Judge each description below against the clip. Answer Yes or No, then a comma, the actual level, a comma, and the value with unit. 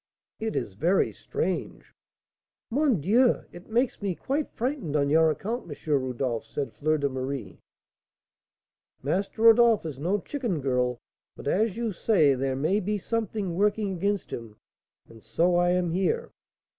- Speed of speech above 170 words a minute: No, average, 150 wpm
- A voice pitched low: No, medium, 180 Hz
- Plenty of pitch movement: Yes, wide, 7.7 semitones